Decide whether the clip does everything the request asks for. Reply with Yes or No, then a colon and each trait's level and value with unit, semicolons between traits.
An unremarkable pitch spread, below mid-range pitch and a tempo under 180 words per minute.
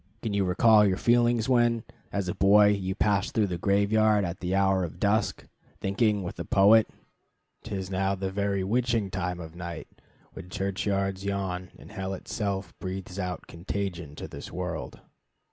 No: narrow, 2.0 semitones; very low, 95 Hz; average, 170 wpm